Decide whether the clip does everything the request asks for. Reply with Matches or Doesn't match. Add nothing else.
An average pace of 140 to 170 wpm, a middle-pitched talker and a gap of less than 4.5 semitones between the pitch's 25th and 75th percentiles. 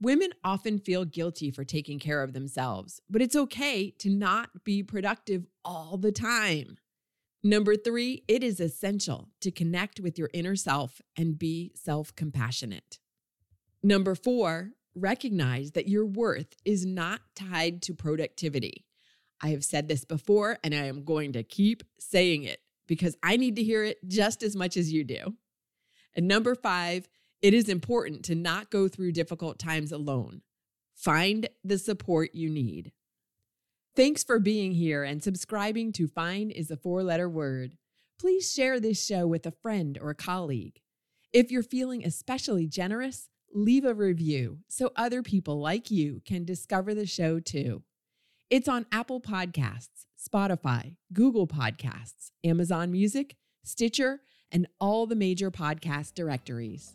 Doesn't match